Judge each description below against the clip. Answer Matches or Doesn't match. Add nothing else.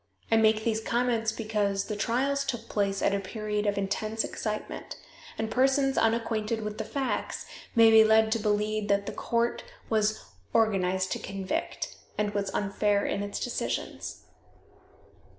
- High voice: Matches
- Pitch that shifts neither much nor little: Doesn't match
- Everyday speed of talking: Matches